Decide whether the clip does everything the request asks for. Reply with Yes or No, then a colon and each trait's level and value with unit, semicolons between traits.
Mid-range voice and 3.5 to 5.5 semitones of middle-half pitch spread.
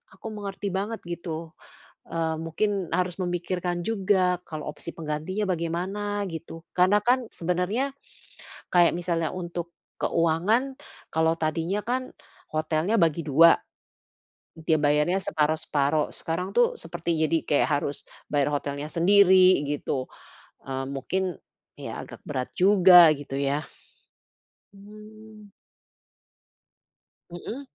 Yes: medium, 175 Hz; average, 3.8 semitones